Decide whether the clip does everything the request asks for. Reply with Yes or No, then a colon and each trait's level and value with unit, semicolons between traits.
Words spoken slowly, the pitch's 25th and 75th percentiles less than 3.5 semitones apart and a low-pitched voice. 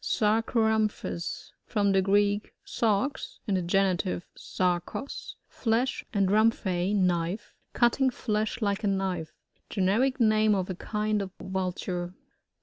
No: slow, 125 wpm; average, 2.8 semitones; high, 200 Hz